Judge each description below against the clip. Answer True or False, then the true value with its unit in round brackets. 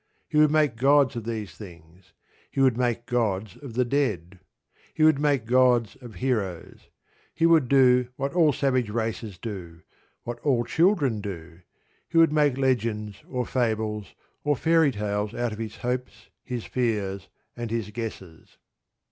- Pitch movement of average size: True (4.4 semitones)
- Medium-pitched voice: False (120 Hz)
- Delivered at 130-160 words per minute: True (155 wpm)